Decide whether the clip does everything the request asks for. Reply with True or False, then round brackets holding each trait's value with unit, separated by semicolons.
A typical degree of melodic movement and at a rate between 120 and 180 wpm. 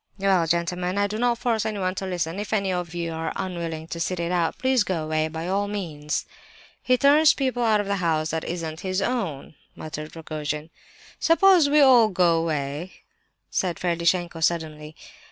True (4.2 semitones; 170 wpm)